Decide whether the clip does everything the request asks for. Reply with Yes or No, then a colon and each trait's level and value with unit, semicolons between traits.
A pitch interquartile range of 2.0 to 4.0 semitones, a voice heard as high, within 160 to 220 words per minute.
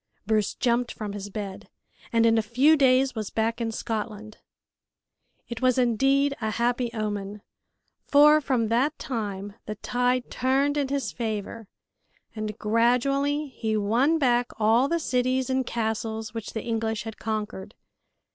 No: average, 3.2 semitones; high, 230 Hz; average, 145 wpm